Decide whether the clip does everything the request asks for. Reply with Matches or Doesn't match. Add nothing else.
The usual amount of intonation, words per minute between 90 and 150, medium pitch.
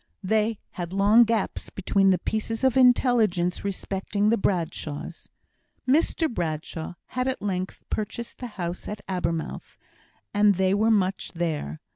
Doesn't match